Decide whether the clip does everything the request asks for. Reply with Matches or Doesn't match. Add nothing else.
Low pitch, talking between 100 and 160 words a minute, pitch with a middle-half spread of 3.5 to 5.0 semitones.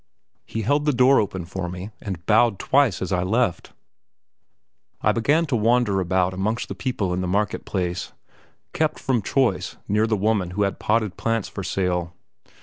Doesn't match